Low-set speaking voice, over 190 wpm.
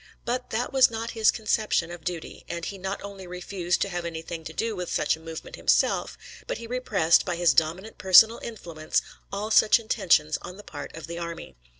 No: medium, 180 Hz; fast, 205 wpm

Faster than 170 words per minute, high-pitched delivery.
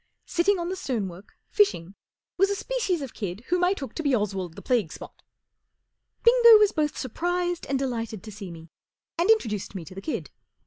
Yes: average, 190 wpm; very high, 270 Hz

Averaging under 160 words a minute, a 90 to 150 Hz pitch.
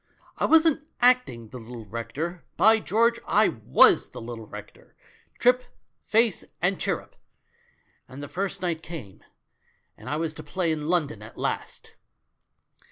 No: average, 150 wpm; medium, 165 Hz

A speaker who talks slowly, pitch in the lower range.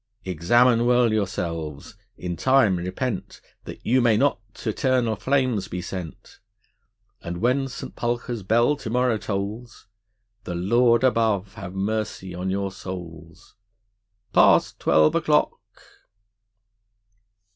Yes: slow, 115 wpm; low, 110 Hz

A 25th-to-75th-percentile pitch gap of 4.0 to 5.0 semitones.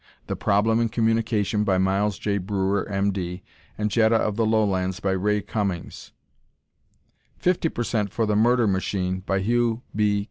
No: narrow, 2.5 semitones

